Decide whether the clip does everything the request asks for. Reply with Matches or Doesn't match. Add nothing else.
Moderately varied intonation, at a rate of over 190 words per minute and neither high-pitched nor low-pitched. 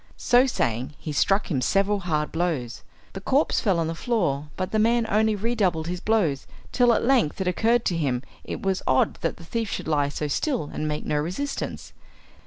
Doesn't match